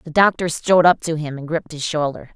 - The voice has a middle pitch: Yes, medium, 160 Hz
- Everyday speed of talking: No, fast, 255 wpm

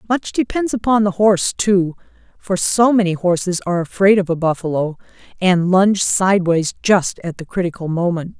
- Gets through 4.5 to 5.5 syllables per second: Yes, 5.2 syllables/s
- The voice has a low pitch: No, medium, 185 Hz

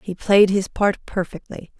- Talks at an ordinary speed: Yes, average, 170 wpm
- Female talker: Yes, female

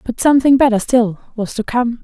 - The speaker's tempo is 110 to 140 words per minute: No, fast, 205 wpm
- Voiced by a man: No, female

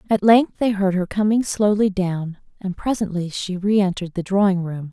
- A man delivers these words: No, female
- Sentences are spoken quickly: No, average, 185 wpm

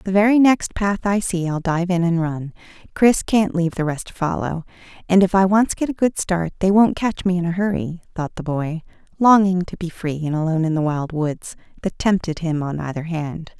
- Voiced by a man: No, female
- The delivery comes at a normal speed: No, fast, 230 wpm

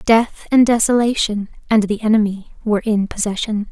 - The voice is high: Yes, high, 215 Hz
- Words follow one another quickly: No, average, 145 wpm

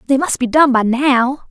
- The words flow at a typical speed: No, fast, 240 wpm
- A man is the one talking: No, female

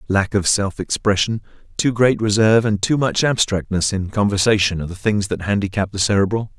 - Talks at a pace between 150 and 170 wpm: No, average, 180 wpm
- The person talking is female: No, male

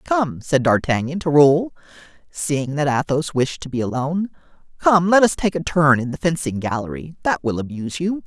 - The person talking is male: Yes, male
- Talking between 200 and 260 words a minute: No, average, 190 wpm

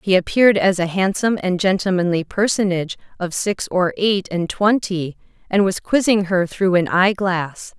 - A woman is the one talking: Yes, female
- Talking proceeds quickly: No, average, 170 wpm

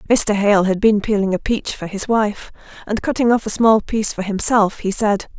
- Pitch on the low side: No, high, 210 Hz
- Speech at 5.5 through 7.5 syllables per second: No, 5.0 syllables/s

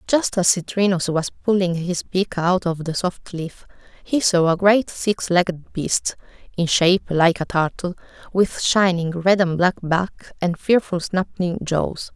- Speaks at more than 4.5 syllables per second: No, 4.1 syllables/s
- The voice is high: No, medium, 180 Hz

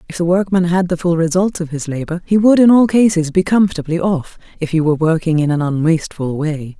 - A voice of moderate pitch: Yes, medium, 170 Hz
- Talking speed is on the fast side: Yes, fast, 230 wpm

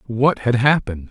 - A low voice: Yes, low, 120 Hz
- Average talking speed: Yes, average, 165 wpm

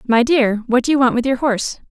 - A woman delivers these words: Yes, female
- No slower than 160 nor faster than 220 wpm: No, fast, 285 wpm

